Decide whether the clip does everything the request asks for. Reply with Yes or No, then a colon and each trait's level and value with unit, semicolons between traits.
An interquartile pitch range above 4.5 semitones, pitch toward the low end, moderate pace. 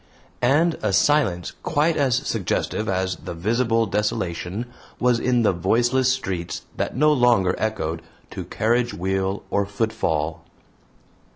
No: average, 4.9 semitones; low, 110 Hz; slow, 125 wpm